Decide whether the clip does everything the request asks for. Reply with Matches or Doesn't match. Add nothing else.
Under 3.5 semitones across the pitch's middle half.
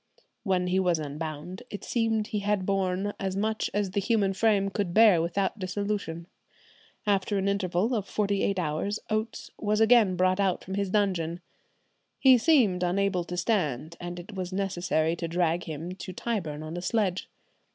Matches